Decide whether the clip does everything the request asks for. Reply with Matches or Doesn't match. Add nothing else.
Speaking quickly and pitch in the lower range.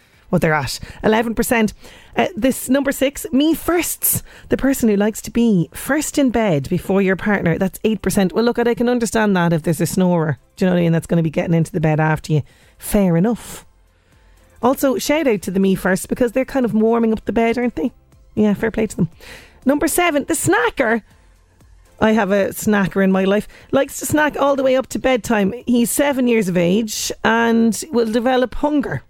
Doesn't match